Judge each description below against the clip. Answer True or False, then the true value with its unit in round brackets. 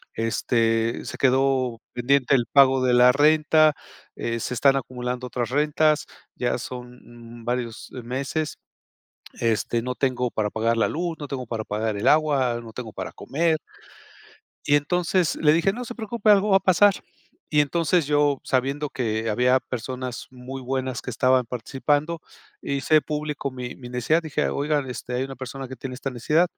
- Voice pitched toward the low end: True (130 Hz)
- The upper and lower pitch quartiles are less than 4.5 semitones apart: True (3.5 semitones)